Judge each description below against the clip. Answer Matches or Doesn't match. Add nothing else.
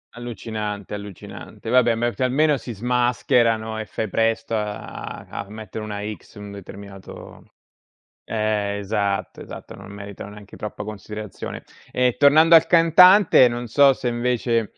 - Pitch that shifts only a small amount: Doesn't match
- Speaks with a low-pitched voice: Matches